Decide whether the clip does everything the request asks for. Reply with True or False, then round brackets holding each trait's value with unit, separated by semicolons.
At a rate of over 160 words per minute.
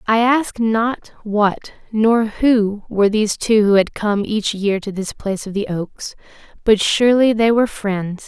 True (180 wpm)